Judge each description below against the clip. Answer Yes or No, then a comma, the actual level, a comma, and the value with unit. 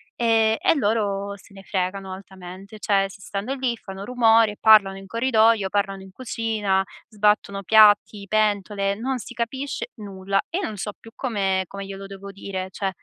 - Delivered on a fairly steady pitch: Yes, narrow, 2.3 semitones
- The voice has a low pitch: No, high, 205 Hz